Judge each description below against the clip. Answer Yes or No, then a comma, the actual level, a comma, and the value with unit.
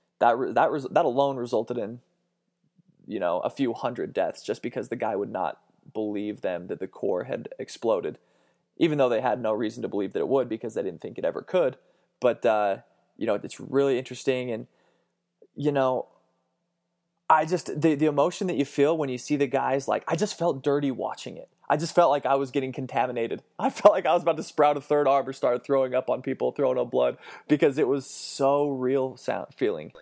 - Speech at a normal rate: No, fast, 220 wpm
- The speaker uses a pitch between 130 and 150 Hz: Yes, medium, 140 Hz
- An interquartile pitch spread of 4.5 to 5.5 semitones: No, average, 4.1 semitones